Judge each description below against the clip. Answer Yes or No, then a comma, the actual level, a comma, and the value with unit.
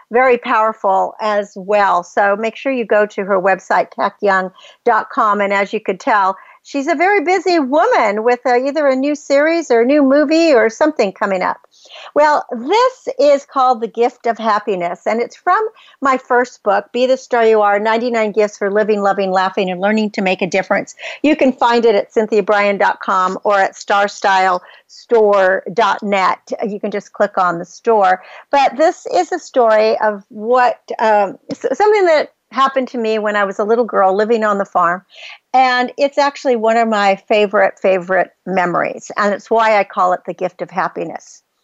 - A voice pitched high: Yes, high, 220 Hz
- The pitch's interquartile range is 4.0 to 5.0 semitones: Yes, average, 4.7 semitones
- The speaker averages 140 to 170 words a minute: No, average, 180 wpm